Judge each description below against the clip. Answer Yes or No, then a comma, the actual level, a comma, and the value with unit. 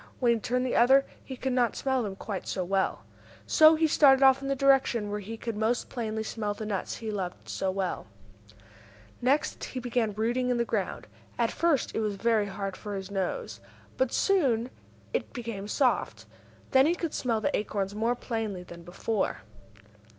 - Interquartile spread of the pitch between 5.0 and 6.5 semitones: No, average, 4.1 semitones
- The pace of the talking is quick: No, average, 190 wpm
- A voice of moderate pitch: No, high, 230 Hz